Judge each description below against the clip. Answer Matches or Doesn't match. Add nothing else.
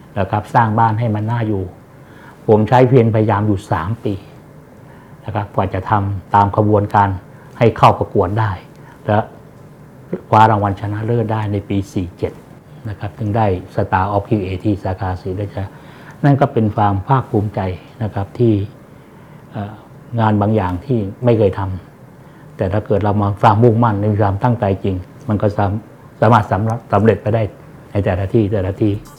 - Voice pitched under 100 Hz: Doesn't match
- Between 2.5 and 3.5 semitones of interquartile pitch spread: Matches